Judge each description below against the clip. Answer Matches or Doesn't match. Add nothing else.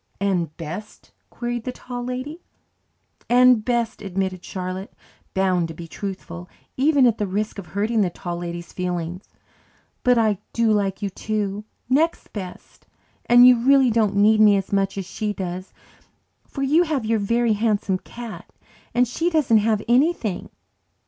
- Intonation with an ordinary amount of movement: Matches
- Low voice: Doesn't match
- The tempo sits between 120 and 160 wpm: Matches